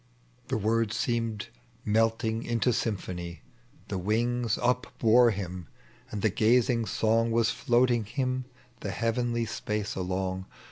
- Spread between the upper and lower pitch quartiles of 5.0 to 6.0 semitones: No, narrow, 2.6 semitones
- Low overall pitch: Yes, low, 115 Hz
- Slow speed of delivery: Yes, slow, 125 wpm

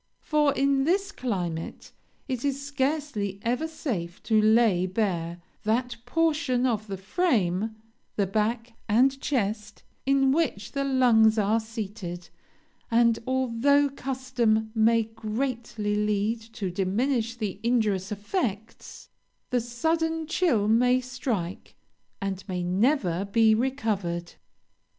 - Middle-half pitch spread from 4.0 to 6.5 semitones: Yes, average, 4.5 semitones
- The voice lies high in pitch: Yes, high, 230 Hz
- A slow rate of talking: Yes, slow, 115 wpm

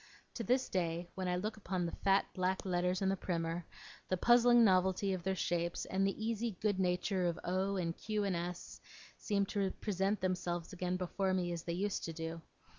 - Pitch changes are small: Yes, narrow, 2.1 semitones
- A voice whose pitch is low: No, medium, 185 Hz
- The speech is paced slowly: No, average, 200 wpm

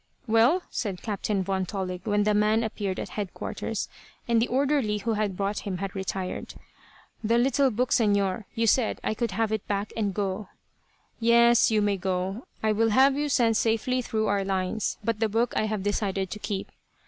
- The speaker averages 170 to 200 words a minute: Yes, average, 190 wpm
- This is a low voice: No, high, 215 Hz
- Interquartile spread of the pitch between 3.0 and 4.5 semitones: No, narrow, 2.6 semitones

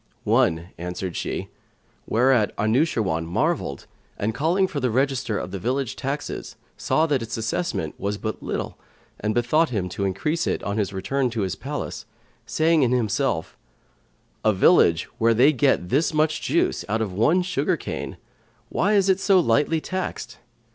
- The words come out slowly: No, average, 160 wpm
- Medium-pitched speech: No, low, 120 Hz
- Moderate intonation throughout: No, wide, 7.1 semitones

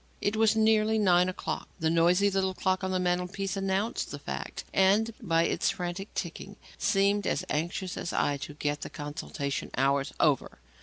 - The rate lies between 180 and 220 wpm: No, average, 170 wpm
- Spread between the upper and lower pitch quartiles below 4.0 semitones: Yes, average, 3.3 semitones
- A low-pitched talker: No, medium, 185 Hz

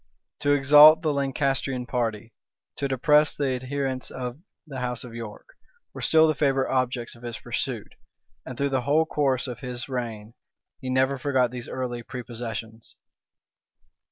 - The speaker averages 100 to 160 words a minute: Yes, average, 155 wpm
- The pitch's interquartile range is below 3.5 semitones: Yes, narrow, 2.5 semitones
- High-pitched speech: No, low, 130 Hz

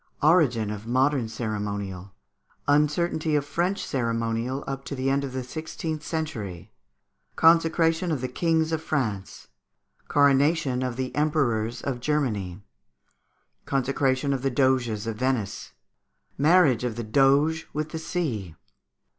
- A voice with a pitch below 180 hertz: Yes, low, 135 Hz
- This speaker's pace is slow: Yes, slow, 130 wpm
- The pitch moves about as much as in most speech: Yes, average, 4.9 semitones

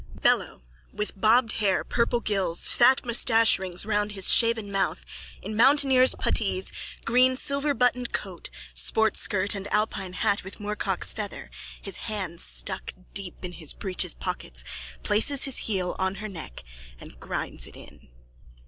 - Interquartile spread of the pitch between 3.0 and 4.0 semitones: Yes, average, 3.7 semitones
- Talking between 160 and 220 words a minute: No, average, 150 wpm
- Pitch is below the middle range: No, high, 210 Hz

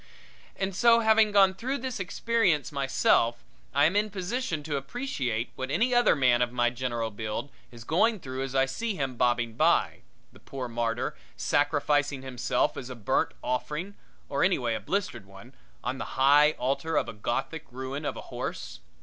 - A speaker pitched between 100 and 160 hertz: Yes, medium, 140 Hz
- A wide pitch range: Yes, wide, 7.4 semitones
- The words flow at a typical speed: Yes, average, 175 wpm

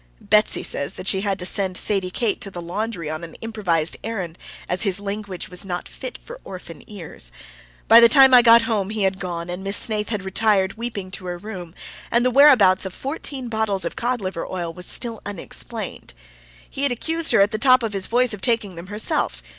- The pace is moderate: No, fast, 215 wpm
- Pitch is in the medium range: No, high, 200 Hz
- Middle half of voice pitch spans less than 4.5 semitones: Yes, average, 3.9 semitones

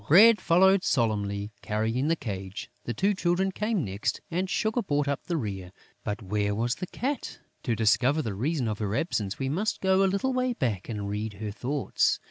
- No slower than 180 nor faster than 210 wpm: Yes, average, 195 wpm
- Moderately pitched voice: No, low, 130 Hz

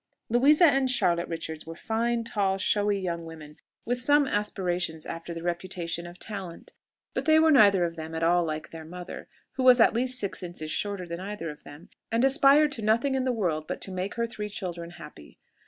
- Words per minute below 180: No, fast, 205 wpm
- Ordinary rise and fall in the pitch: No, wide, 5.8 semitones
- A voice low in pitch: No, high, 190 Hz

